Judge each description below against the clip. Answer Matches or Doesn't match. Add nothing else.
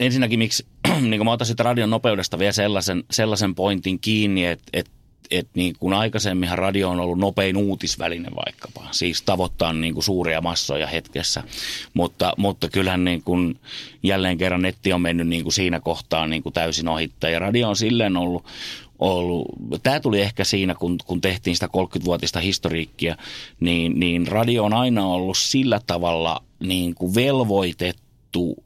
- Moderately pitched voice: Doesn't match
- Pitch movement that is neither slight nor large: Matches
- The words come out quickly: Matches